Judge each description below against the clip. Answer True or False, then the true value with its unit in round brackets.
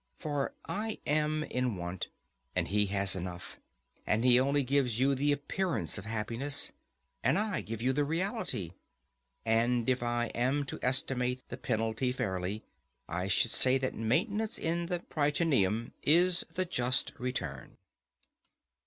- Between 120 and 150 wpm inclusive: True (145 wpm)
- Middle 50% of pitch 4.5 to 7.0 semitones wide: True (4.8 semitones)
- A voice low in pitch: True (125 Hz)